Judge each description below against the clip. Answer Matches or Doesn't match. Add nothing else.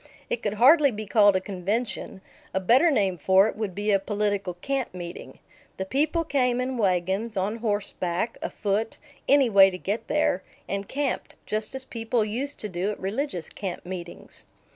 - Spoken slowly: Doesn't match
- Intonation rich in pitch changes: Doesn't match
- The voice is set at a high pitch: Matches